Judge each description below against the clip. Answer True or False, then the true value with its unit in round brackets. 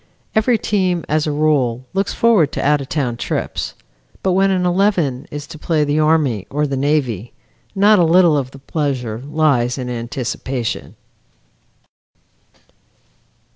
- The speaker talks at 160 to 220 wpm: False (145 wpm)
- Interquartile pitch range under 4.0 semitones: False (5.2 semitones)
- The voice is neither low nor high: True (150 Hz)